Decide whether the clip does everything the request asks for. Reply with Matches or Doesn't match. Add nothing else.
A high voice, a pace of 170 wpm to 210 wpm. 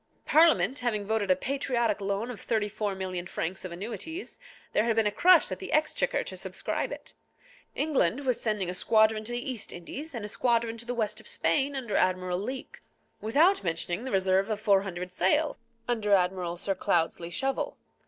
Matches